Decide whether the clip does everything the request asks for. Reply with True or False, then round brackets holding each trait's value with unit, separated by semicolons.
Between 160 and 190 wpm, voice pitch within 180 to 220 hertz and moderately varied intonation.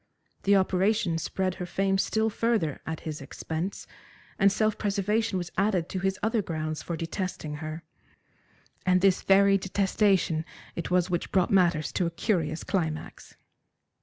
False (150 wpm; 185 Hz; 3.3 semitones)